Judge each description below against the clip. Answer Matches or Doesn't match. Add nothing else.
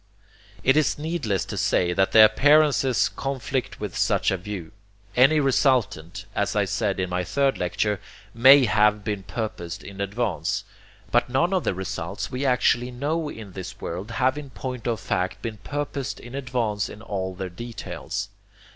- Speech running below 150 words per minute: Doesn't match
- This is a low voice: Matches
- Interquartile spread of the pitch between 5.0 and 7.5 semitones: Matches